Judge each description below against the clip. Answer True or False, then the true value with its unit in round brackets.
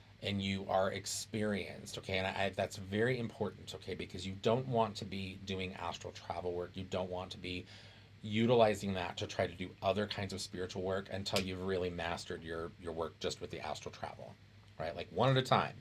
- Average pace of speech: False (215 wpm)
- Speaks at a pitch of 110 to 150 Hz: False (95 Hz)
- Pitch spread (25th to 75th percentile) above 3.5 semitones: False (2.4 semitones)